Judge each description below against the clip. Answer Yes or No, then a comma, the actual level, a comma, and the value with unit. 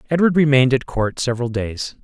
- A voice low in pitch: Yes, low, 130 Hz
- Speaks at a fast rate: No, average, 175 wpm